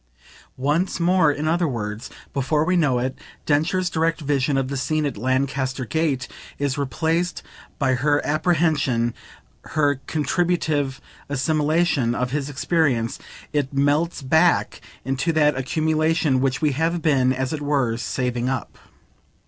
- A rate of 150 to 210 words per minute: No, slow, 135 wpm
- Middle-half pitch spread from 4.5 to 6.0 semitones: No, average, 3.2 semitones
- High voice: No, medium, 145 Hz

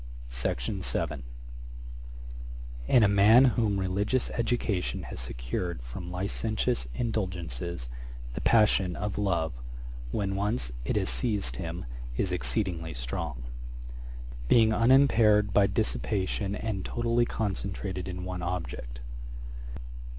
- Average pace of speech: No, slow, 105 wpm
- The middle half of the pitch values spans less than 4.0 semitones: No, average, 4.7 semitones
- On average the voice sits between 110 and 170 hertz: No, very low, 95 Hz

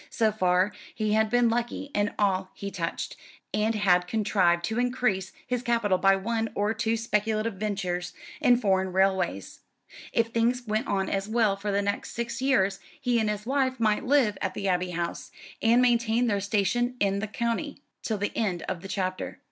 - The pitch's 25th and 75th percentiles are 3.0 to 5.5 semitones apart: Yes, average, 3.3 semitones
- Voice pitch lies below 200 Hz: No, high, 210 Hz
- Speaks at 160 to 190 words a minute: Yes, average, 185 wpm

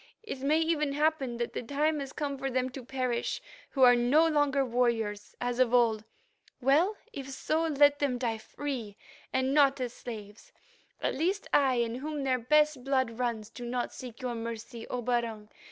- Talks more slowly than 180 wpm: No, average, 185 wpm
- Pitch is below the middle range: No, very high, 255 Hz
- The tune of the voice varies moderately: Yes, average, 3.3 semitones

